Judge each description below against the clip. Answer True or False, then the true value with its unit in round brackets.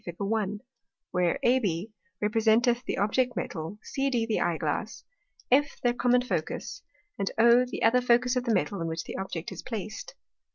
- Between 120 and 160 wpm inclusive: False (170 wpm)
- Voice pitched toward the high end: True (225 Hz)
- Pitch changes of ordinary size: True (4.3 semitones)